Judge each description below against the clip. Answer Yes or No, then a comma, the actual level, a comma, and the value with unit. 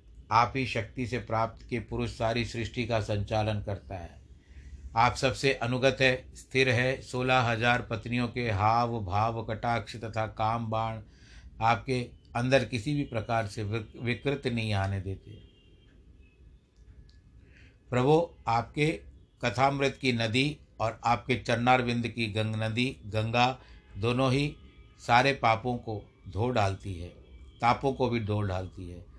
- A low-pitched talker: Yes, low, 115 Hz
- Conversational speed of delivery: Yes, average, 135 wpm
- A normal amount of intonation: Yes, average, 3.1 semitones